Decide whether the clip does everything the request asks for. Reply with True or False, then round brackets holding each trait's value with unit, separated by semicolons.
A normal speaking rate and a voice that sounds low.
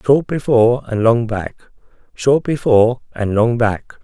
True (150 wpm; 120 Hz)